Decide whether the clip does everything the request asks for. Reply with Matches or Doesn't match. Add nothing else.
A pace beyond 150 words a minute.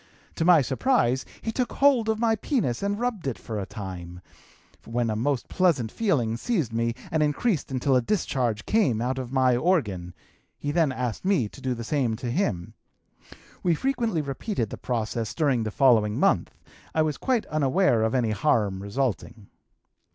Matches